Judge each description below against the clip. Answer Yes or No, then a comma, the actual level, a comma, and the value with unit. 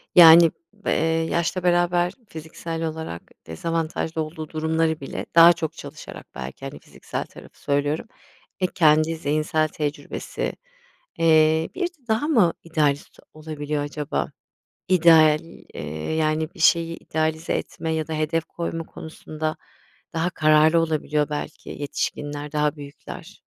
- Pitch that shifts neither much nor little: No, narrow, 1.5 semitones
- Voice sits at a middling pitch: Yes, medium, 160 Hz